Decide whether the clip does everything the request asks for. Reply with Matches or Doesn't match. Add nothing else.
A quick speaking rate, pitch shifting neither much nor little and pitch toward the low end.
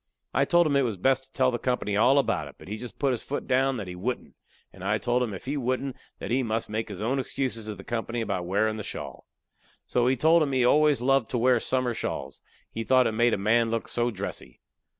Matches